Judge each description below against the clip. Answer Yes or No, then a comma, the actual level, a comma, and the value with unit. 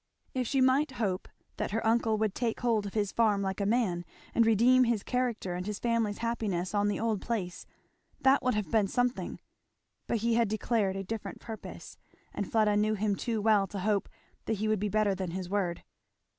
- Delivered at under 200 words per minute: No, fast, 205 wpm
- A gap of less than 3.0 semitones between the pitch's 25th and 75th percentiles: Yes, narrow, 2.6 semitones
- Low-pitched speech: No, high, 215 Hz